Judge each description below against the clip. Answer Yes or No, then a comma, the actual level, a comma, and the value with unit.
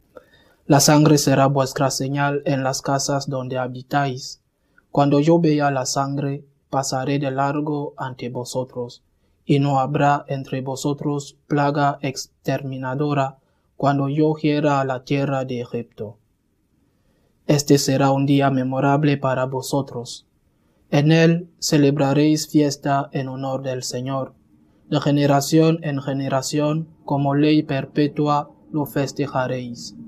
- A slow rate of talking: Yes, slow, 120 wpm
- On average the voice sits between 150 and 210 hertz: No, medium, 140 Hz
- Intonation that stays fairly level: Yes, narrow, 1.8 semitones